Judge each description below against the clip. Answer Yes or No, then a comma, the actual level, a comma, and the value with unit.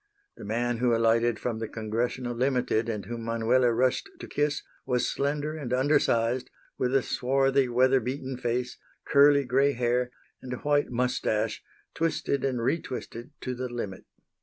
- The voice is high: No, low, 125 Hz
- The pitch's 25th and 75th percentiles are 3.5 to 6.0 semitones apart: No, narrow, 2.4 semitones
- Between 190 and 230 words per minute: No, average, 160 wpm